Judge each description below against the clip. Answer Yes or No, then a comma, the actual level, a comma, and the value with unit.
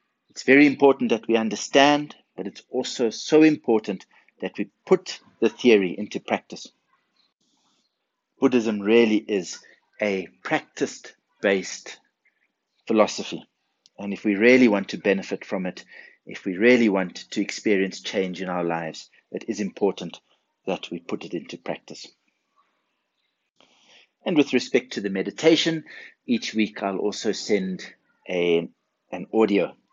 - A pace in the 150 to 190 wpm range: No, slow, 135 wpm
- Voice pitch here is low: Yes, low, 110 Hz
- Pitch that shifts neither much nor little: No, wide, 5.8 semitones